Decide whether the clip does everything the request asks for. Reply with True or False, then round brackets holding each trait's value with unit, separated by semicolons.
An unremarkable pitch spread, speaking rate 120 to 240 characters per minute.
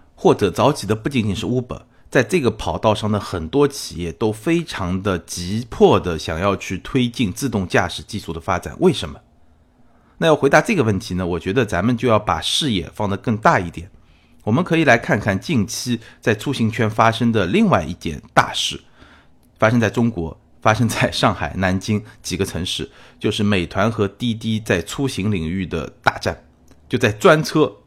False (5.0 semitones; 280 characters per minute)